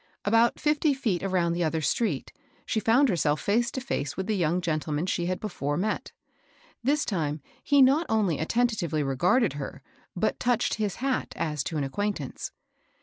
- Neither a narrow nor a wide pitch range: No, wide, 7.1 semitones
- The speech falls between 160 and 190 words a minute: Yes, average, 170 wpm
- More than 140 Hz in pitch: Yes, high, 190 Hz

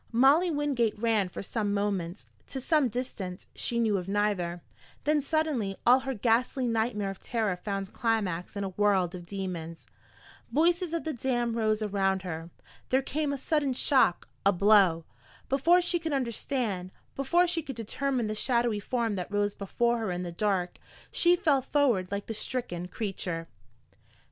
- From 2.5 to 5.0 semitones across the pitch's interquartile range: No, wide, 5.5 semitones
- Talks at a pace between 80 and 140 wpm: No, average, 165 wpm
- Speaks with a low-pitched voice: No, high, 220 Hz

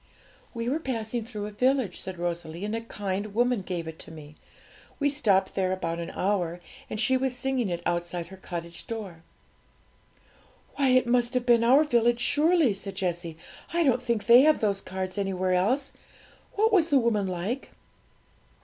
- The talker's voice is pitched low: No, high, 215 Hz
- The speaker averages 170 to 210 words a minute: Yes, average, 175 wpm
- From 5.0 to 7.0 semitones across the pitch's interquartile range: Yes, wide, 5.4 semitones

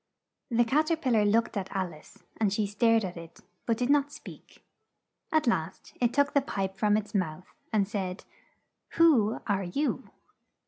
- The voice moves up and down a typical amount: Yes, average, 4.7 semitones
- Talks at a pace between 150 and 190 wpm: Yes, average, 180 wpm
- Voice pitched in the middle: No, high, 215 Hz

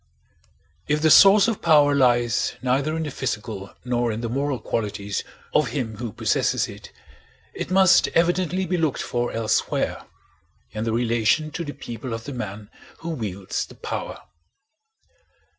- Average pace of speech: Yes, average, 150 wpm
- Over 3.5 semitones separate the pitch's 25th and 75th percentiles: Yes, wide, 5.5 semitones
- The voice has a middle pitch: No, low, 125 Hz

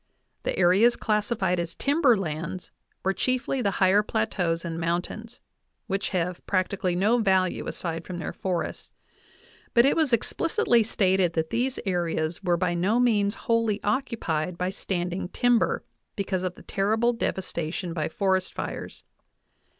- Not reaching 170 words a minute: Yes, average, 145 wpm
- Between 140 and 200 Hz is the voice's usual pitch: Yes, high, 190 Hz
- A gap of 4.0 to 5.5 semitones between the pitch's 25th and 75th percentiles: Yes, average, 4.5 semitones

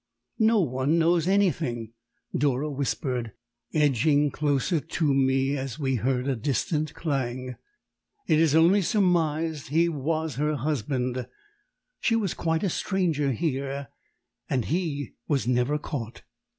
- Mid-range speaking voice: Yes, medium, 145 Hz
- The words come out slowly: Yes, slow, 125 wpm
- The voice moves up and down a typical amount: Yes, average, 3.6 semitones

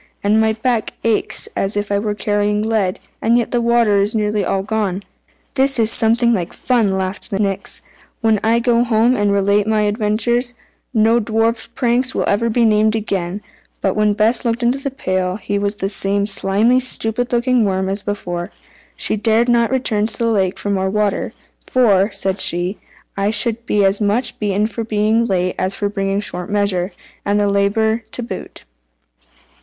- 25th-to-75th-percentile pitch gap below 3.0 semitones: Yes, narrow, 2.5 semitones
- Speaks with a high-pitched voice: Yes, high, 210 Hz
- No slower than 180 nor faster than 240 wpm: Yes, average, 185 wpm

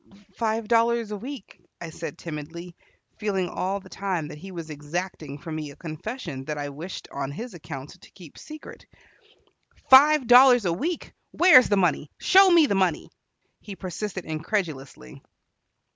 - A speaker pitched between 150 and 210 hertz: Yes, medium, 185 Hz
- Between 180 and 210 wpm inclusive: No, average, 160 wpm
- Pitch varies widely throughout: Yes, wide, 6.6 semitones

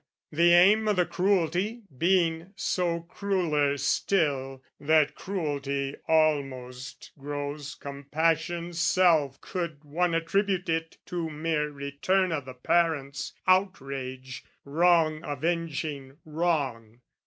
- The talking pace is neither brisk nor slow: No, slow, 100 wpm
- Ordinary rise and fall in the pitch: Yes, average, 3.6 semitones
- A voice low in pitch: No, medium, 160 Hz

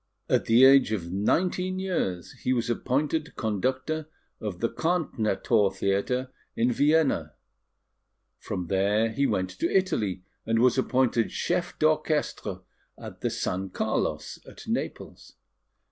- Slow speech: Yes, slow, 125 wpm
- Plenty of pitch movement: Yes, wide, 7.5 semitones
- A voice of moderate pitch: No, low, 120 Hz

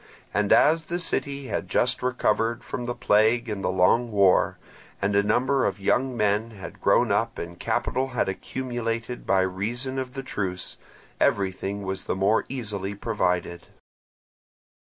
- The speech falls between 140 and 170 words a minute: Yes, average, 155 wpm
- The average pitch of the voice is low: Yes, low, 110 Hz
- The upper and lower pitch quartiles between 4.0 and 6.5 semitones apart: Yes, average, 4.3 semitones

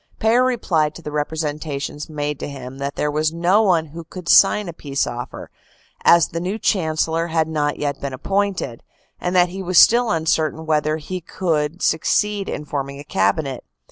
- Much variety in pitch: No, average, 3.5 semitones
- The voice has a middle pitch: Yes, medium, 160 Hz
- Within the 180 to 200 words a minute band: Yes, average, 190 wpm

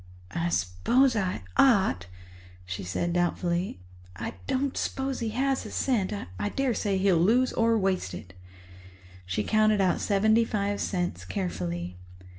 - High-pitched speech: Yes, high, 195 Hz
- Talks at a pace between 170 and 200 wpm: No, slow, 135 wpm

